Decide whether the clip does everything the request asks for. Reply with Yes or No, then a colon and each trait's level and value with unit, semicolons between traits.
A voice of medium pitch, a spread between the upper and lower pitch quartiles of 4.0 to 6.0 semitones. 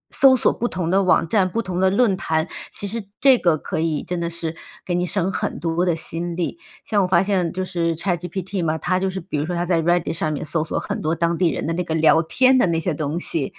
No: medium, 175 Hz; narrow, 2.4 semitones